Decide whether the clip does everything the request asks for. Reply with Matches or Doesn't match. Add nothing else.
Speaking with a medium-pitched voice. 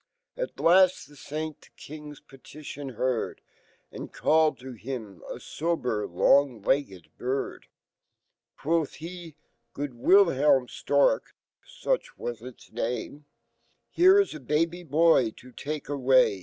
Matches